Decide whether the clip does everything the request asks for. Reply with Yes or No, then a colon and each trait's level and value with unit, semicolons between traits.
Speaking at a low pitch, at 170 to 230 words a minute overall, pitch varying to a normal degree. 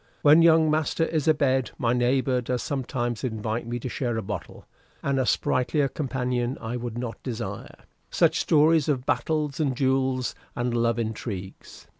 No: low, 125 Hz; average, 160 wpm; average, 3.0 semitones